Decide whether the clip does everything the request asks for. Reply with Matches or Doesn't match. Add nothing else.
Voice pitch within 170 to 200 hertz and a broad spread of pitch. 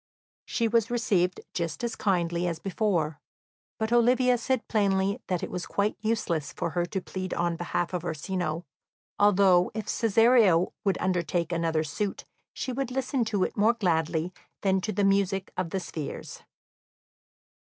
Doesn't match